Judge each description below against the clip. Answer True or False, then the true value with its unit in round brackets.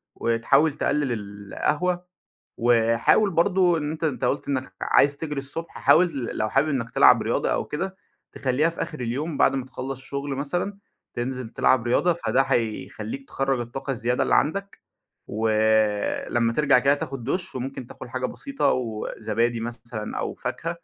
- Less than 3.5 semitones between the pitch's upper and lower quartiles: False (4.5 semitones)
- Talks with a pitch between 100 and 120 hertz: False (135 Hz)